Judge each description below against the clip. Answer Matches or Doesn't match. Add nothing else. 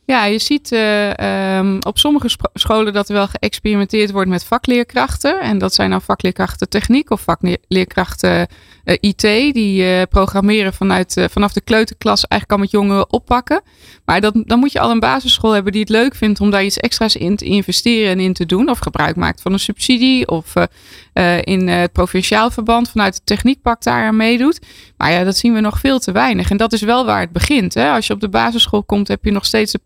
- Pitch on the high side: Matches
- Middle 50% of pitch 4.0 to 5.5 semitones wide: Doesn't match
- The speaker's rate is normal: Doesn't match